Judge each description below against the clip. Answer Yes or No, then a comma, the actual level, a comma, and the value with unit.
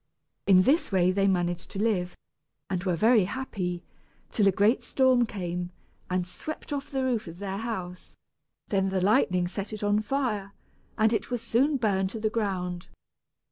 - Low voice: No, high, 200 Hz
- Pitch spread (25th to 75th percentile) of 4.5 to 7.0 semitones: No, average, 4.0 semitones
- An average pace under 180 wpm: Yes, average, 170 wpm